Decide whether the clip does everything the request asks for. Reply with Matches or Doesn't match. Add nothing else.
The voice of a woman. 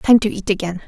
Matches